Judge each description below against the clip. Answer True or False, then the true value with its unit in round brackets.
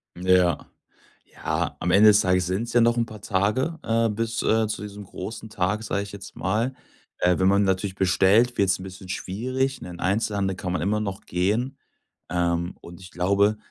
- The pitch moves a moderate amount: True (3.2 semitones)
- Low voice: True (100 Hz)